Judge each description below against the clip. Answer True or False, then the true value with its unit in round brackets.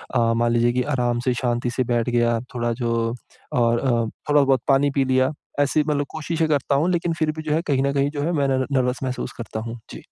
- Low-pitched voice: True (130 Hz)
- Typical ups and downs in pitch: True (3.2 semitones)